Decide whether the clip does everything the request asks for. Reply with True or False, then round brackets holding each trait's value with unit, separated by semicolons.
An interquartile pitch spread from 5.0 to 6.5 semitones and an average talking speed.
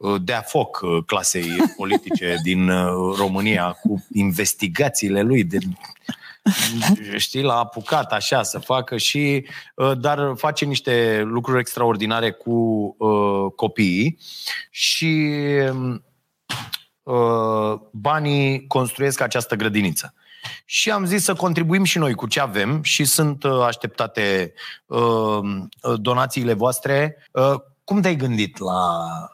False (5.4 semitones; 105 wpm)